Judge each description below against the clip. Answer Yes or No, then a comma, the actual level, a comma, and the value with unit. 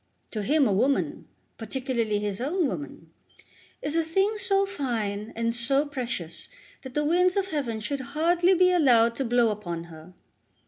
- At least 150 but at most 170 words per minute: Yes, average, 165 wpm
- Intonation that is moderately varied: No, wide, 7.1 semitones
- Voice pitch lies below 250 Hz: No, very high, 260 Hz